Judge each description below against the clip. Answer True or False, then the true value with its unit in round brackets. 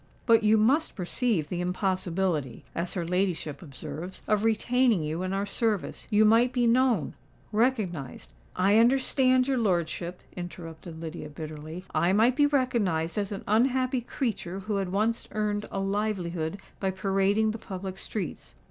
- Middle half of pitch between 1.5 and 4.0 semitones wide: False (4.5 semitones)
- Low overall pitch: False (195 Hz)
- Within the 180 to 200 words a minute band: False (150 wpm)